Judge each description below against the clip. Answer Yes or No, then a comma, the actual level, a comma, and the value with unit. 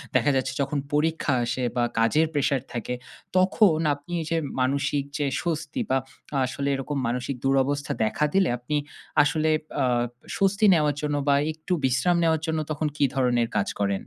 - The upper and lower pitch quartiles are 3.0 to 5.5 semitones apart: Yes, average, 3.4 semitones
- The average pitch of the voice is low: No, medium, 145 Hz